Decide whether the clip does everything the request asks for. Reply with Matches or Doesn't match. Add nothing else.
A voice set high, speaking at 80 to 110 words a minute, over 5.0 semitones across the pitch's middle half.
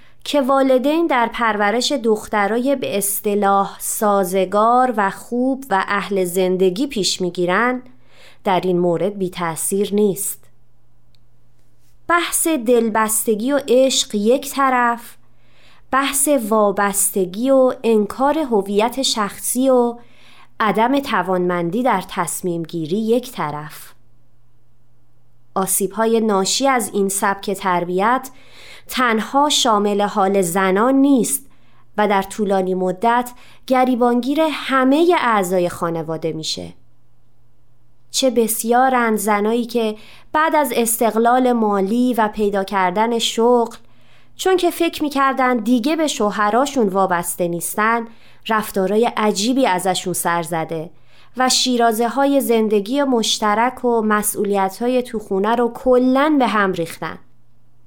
Matches